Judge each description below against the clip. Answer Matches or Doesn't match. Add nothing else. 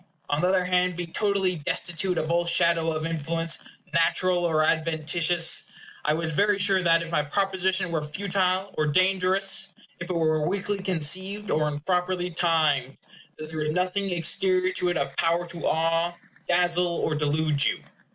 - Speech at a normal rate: Matches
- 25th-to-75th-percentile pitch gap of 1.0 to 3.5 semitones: Matches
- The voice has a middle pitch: Matches